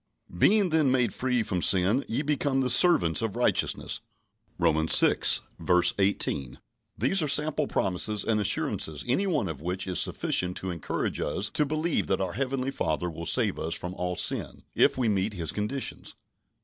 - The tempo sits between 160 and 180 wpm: Yes, average, 170 wpm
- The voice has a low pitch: Yes, low, 105 Hz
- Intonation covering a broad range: Yes, wide, 7.2 semitones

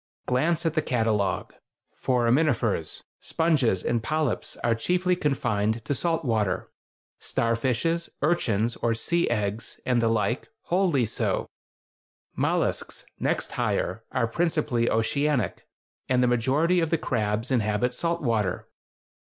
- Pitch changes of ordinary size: No, wide, 5.8 semitones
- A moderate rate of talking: No, slow, 120 wpm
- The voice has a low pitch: Yes, low, 125 Hz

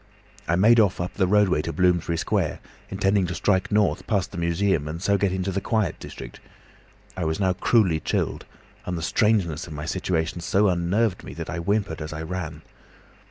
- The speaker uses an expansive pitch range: No, average, 3.3 semitones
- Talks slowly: No, average, 195 wpm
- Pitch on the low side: Yes, very low, 90 Hz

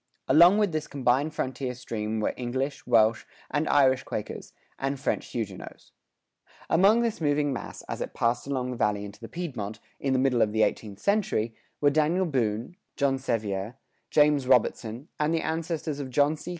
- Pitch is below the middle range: Yes, low, 130 Hz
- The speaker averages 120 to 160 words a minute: No, average, 175 wpm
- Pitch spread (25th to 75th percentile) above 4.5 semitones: Yes, average, 4.9 semitones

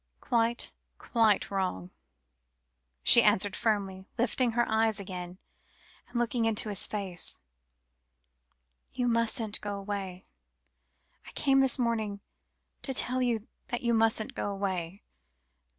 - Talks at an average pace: No, slow, 120 wpm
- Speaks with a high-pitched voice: Yes, high, 220 Hz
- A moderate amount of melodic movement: Yes, average, 3.2 semitones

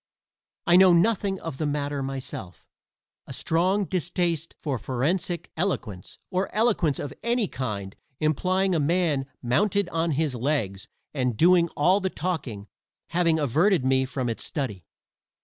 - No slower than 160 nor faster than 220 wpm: No, average, 140 wpm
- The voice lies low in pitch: No, medium, 160 Hz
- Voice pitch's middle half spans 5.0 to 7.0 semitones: Yes, wide, 5.6 semitones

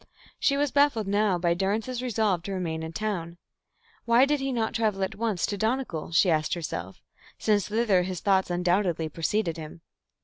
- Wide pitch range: No, average, 4.7 semitones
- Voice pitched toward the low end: No, high, 195 Hz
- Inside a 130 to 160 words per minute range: No, average, 175 wpm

